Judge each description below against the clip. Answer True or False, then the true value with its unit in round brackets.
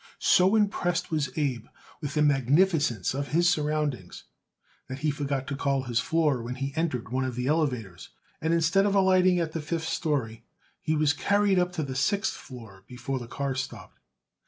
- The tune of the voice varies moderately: True (4.2 semitones)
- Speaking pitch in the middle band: True (145 Hz)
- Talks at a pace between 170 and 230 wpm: True (180 wpm)